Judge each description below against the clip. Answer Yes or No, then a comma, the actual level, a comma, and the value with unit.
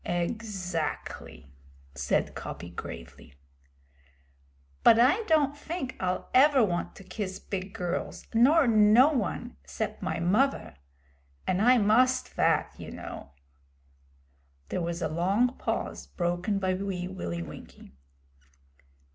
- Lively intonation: Yes, wide, 6.1 semitones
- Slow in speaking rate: Yes, slow, 115 wpm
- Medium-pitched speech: No, high, 195 Hz